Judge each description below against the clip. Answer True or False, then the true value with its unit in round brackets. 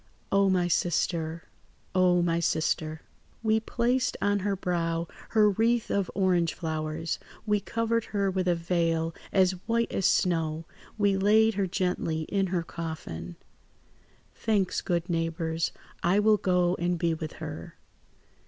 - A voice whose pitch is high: False (180 Hz)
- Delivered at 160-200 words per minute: False (135 wpm)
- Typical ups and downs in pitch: True (3.4 semitones)